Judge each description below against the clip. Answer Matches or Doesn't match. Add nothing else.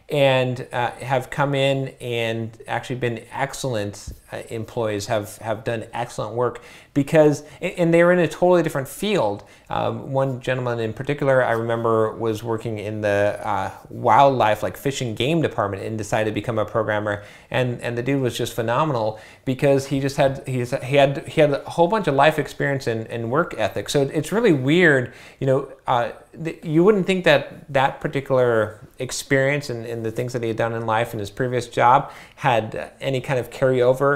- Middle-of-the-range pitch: Doesn't match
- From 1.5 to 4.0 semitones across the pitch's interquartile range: Matches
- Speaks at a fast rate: Doesn't match